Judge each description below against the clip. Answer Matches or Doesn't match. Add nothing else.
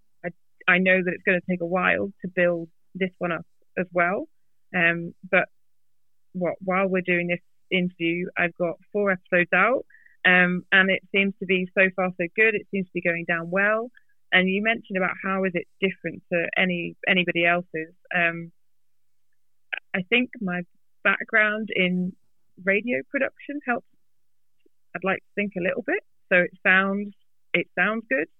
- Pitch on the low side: Doesn't match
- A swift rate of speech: Doesn't match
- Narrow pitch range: Matches